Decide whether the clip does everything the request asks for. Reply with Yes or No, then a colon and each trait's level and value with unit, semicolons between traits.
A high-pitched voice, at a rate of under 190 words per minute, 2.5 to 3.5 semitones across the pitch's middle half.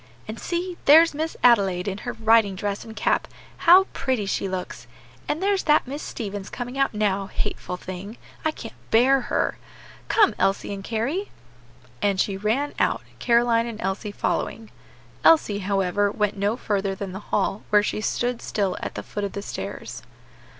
No: high, 215 Hz; average, 170 wpm; average, 4.1 semitones